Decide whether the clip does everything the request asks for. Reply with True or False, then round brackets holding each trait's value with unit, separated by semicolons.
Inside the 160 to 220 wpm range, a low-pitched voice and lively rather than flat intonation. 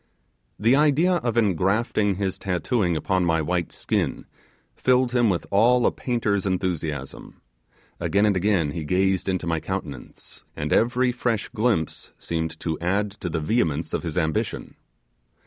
False (145 wpm; 95 Hz; 5.7 semitones)